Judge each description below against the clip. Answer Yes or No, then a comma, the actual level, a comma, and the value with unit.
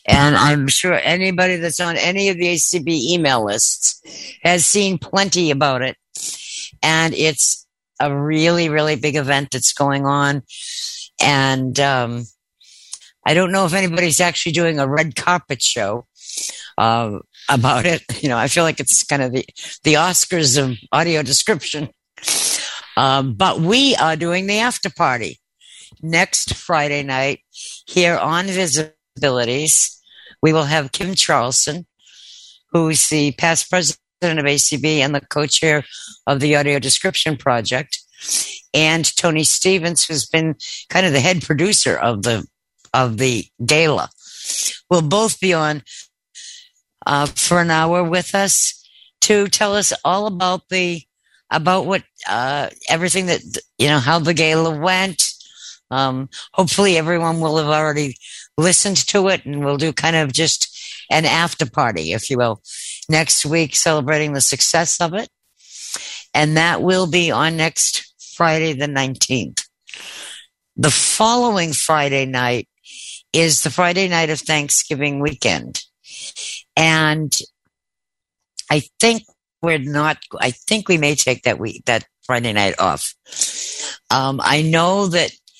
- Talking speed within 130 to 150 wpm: Yes, average, 140 wpm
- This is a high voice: No, medium, 155 Hz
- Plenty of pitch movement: No, average, 4.0 semitones